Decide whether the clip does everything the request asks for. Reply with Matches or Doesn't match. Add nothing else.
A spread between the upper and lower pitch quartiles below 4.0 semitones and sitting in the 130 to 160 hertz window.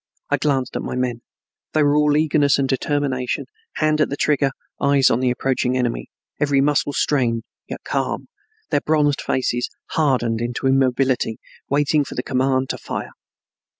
Matches